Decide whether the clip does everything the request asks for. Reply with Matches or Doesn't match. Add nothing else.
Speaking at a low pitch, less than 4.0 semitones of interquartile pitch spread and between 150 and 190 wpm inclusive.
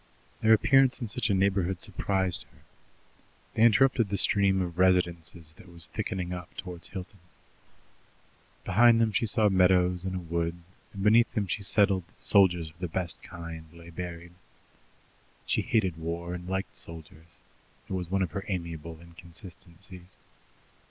Matches